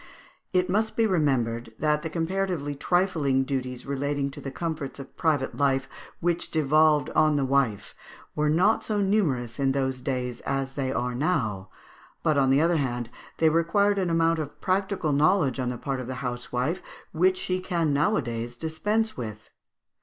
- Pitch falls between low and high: Yes, medium, 145 Hz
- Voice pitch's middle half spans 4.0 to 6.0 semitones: Yes, average, 4.6 semitones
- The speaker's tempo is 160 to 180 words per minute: Yes, average, 170 wpm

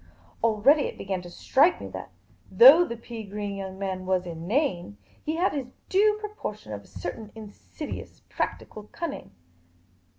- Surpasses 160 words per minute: No, average, 155 wpm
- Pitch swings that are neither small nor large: No, wide, 8.0 semitones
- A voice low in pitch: No, high, 215 Hz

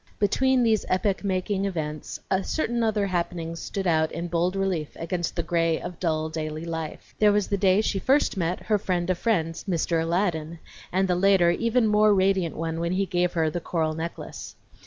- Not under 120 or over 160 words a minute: No, average, 190 wpm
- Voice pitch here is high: No, medium, 180 Hz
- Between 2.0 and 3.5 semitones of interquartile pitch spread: Yes, average, 3.2 semitones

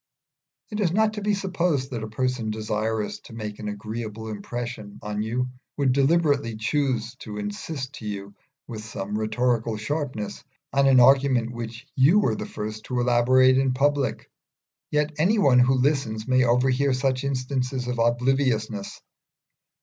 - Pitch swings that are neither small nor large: Yes, average, 3.9 semitones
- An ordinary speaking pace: Yes, average, 155 wpm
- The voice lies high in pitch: No, low, 125 Hz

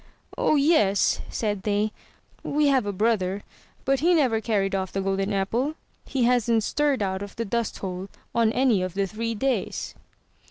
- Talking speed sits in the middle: Yes, average, 170 wpm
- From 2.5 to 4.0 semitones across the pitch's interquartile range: No, average, 4.5 semitones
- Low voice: No, high, 220 Hz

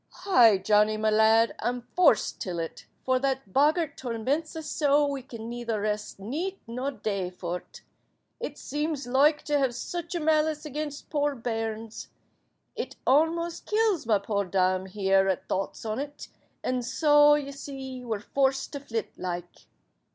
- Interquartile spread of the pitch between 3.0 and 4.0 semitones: No, wide, 5.5 semitones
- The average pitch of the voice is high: Yes, very high, 255 Hz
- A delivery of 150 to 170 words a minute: Yes, average, 155 wpm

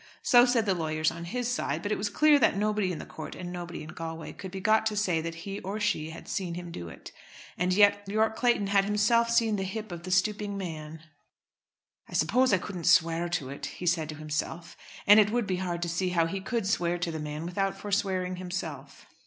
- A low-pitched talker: No, medium, 185 Hz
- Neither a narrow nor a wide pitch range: Yes, average, 3.8 semitones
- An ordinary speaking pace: No, fast, 235 wpm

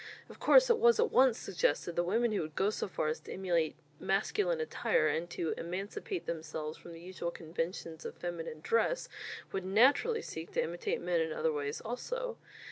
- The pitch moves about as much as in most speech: No, wide, 7.9 semitones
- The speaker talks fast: No, average, 190 wpm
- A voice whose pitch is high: No, medium, 180 Hz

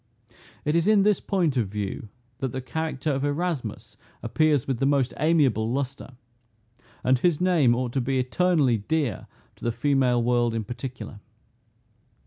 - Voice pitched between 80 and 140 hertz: Yes, low, 135 Hz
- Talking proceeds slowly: No, average, 155 wpm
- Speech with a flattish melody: No, average, 4.5 semitones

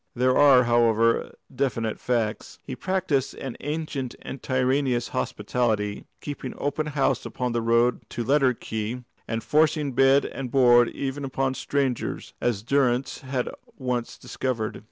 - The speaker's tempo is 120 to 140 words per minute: Yes, slow, 135 wpm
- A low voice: Yes, low, 125 Hz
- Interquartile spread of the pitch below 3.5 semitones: Yes, narrow, 2.6 semitones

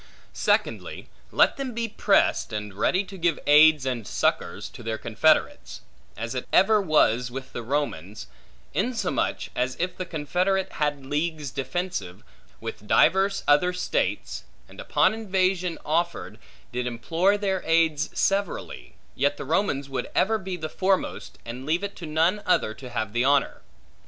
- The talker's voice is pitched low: No, medium, 155 Hz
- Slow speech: No, average, 150 wpm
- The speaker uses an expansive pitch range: Yes, wide, 6.7 semitones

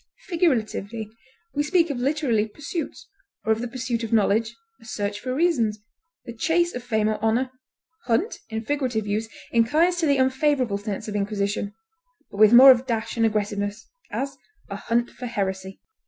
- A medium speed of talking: Yes, average, 170 wpm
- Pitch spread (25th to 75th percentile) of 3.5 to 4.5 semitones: Yes, average, 3.9 semitones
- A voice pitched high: Yes, high, 230 Hz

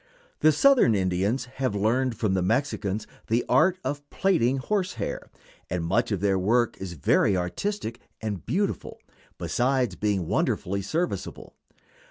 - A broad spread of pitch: Yes, wide, 6.6 semitones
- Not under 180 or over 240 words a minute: No, average, 140 wpm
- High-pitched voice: No, low, 115 Hz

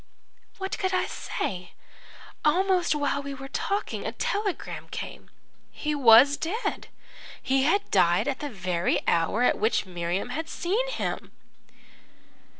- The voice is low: No, very high, 280 Hz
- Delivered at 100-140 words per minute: Yes, slow, 135 wpm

